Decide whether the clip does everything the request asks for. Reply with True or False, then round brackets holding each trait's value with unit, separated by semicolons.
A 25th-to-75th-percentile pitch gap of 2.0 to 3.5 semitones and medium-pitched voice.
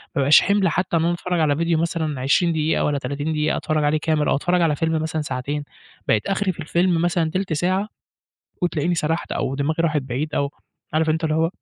True (2.4 semitones; 160 Hz)